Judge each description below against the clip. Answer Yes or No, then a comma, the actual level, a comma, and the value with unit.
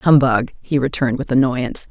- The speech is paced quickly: No, average, 160 wpm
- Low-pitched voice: Yes, low, 130 Hz